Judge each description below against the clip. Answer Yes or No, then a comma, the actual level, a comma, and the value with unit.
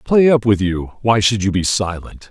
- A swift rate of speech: Yes, fast, 235 wpm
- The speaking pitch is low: Yes, low, 105 Hz